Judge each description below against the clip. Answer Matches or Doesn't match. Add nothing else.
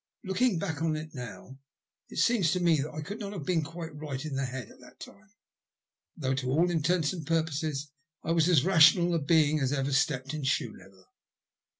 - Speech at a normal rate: Doesn't match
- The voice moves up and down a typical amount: Matches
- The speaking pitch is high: Doesn't match